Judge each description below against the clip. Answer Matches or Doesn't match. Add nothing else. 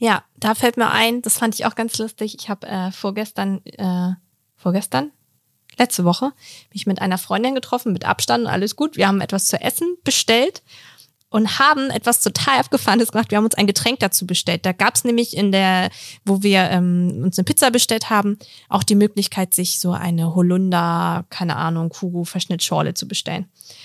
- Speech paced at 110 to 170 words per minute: Doesn't match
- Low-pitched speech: Doesn't match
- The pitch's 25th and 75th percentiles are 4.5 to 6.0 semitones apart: Doesn't match